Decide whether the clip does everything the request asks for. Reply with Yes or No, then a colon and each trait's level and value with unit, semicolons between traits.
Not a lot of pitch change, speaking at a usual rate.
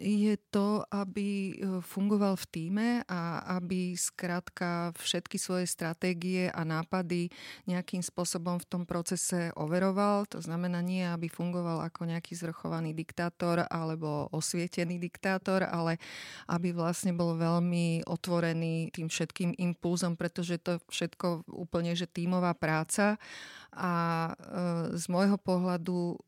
Yes: narrow, 1.4 semitones; average, 125 wpm